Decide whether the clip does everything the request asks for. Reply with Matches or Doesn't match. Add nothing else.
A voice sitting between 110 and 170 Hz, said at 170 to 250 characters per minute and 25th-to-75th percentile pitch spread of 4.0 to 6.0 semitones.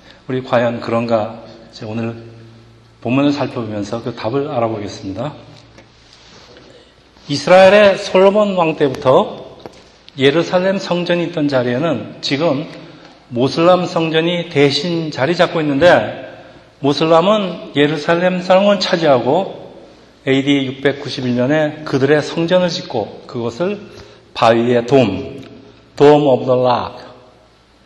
Matches